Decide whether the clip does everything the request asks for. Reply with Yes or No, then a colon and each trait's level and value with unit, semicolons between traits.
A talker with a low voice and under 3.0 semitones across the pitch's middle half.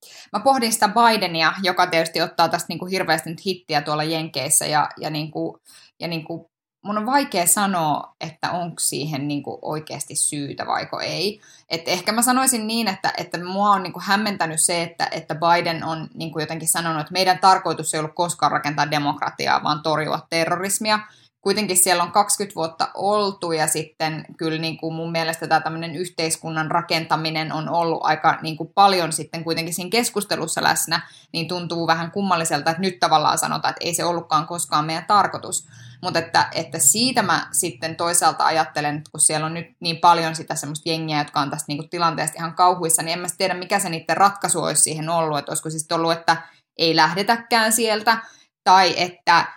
No: medium, 165 Hz; narrow, 2.5 semitones